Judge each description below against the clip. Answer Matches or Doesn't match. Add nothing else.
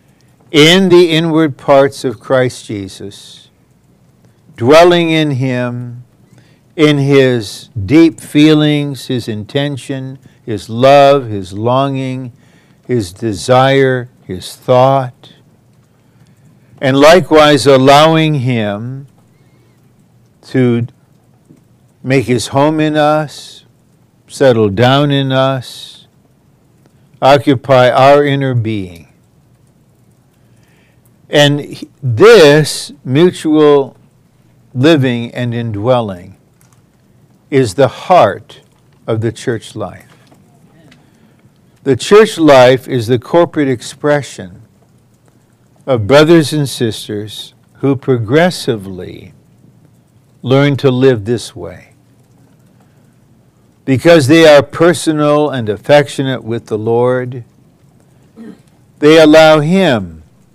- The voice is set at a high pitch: Doesn't match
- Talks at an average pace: Doesn't match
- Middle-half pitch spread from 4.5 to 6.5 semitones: Doesn't match